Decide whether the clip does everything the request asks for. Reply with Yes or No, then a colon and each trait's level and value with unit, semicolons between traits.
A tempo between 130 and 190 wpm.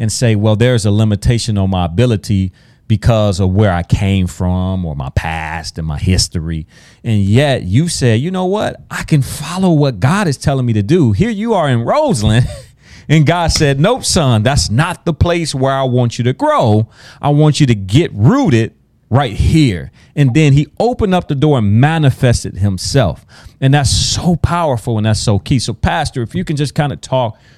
No: average, 200 wpm